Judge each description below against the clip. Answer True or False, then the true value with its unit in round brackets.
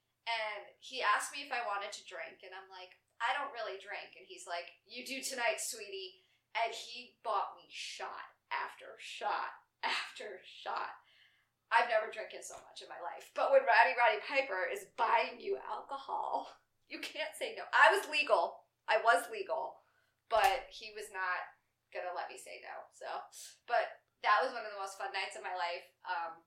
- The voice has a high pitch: True (225 Hz)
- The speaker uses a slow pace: False (190 wpm)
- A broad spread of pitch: True (6.0 semitones)